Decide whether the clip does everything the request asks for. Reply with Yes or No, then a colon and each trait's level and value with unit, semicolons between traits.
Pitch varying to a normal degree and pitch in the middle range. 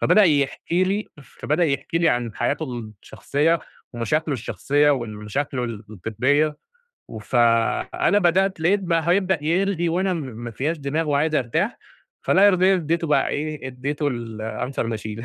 No: wide, 5.7 semitones; medium, 150 Hz